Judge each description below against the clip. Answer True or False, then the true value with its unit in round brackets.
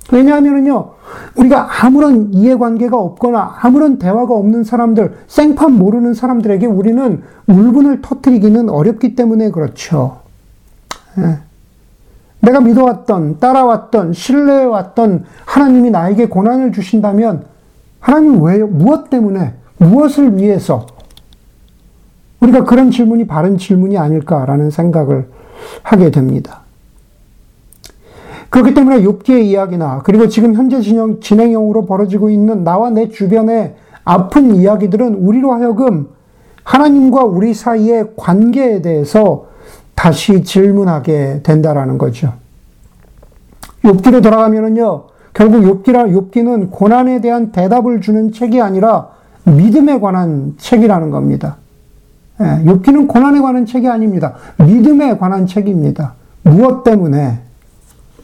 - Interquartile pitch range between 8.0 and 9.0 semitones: False (5.6 semitones)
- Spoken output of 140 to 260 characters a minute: False (285 characters per minute)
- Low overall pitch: False (215 Hz)